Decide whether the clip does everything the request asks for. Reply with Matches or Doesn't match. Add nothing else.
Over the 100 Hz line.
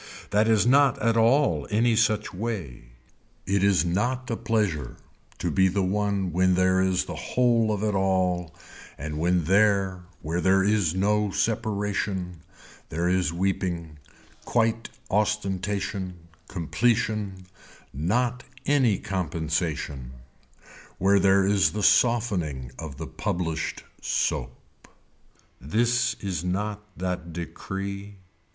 Doesn't match